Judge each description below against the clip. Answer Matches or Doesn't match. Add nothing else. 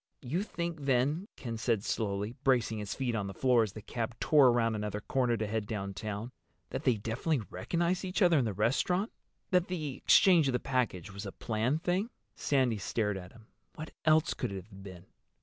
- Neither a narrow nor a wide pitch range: Doesn't match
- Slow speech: Doesn't match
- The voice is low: Matches